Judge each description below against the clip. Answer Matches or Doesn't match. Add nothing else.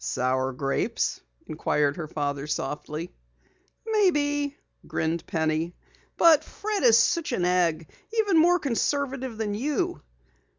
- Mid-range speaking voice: Doesn't match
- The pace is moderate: Doesn't match